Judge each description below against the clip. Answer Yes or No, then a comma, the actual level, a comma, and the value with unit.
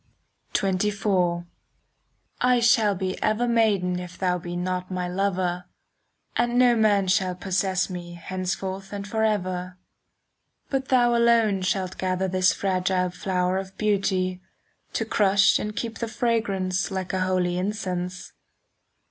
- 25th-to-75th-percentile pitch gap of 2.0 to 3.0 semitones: Yes, narrow, 2.5 semitones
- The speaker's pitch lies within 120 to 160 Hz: No, high, 190 Hz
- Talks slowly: Yes, slow, 130 wpm